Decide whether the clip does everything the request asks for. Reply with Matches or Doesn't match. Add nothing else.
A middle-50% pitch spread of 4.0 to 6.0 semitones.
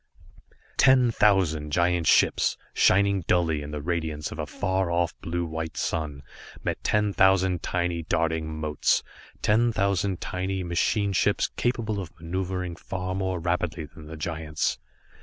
Doesn't match